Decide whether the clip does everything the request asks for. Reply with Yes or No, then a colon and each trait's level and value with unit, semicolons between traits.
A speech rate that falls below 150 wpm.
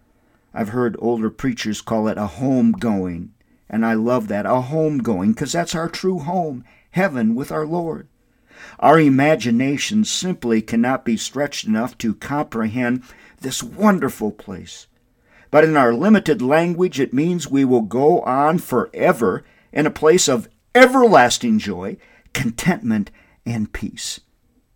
Yes: average, 140 wpm